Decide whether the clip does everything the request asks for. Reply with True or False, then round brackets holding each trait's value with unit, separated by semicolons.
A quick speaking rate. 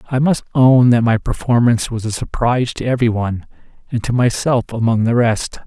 False (170 wpm)